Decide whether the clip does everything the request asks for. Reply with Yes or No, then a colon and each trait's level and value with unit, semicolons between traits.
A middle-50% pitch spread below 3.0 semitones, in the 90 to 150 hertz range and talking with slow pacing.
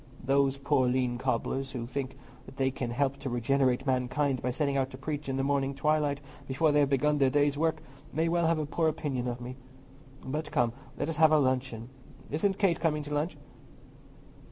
No: narrow, 2.4 semitones; medium, 140 Hz; average, 195 wpm